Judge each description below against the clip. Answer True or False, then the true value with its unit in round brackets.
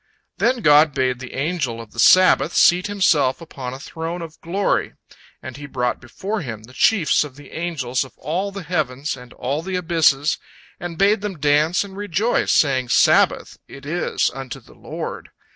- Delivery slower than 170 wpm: False (175 wpm)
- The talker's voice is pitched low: False (155 Hz)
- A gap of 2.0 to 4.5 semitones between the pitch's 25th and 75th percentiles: False (5.3 semitones)